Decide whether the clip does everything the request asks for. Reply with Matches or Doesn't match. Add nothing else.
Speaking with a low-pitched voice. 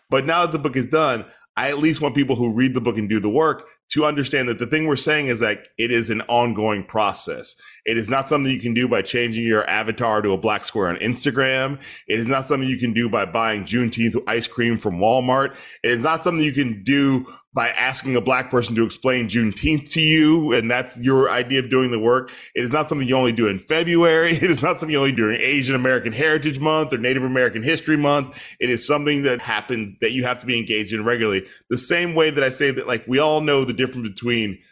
Matches